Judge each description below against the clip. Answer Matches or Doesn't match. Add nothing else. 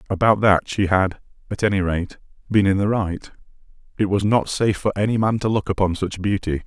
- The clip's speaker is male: Matches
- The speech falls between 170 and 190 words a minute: Doesn't match